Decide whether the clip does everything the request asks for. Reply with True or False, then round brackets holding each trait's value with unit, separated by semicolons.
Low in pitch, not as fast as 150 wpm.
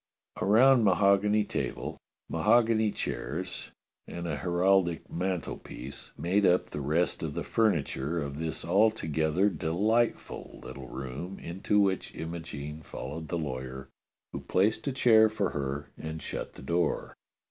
True (85 Hz; 135 wpm)